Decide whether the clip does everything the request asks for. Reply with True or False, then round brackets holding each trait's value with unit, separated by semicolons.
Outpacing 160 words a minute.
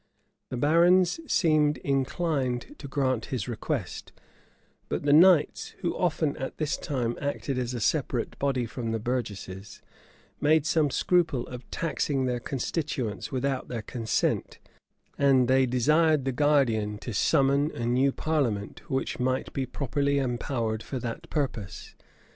False (140 wpm)